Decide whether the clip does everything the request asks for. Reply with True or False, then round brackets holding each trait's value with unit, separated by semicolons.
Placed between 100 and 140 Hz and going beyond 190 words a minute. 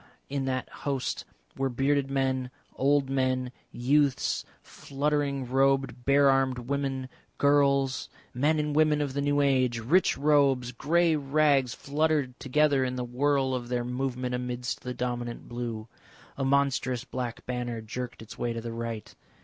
False (135 Hz; 150 wpm)